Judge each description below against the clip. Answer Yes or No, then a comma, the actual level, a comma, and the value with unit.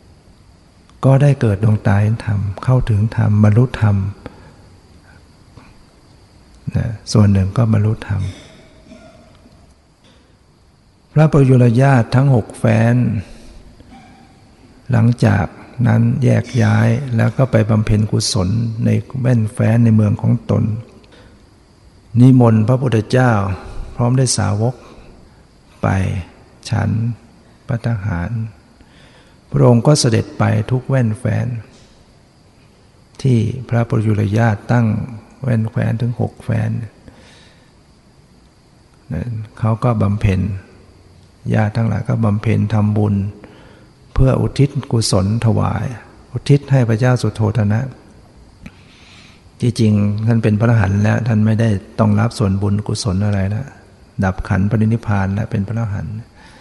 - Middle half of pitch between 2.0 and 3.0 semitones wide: Yes, average, 2.7 semitones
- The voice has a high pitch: No, low, 110 Hz